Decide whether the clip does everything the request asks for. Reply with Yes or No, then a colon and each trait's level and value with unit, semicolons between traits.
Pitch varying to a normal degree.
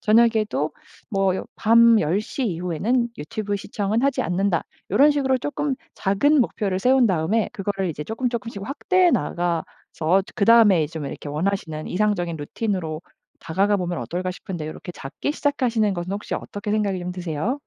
Yes: average, 4.8 semitones